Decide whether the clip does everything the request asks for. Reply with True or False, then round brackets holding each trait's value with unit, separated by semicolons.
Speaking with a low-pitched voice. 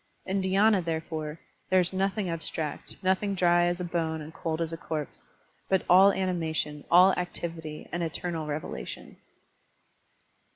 False (175 Hz)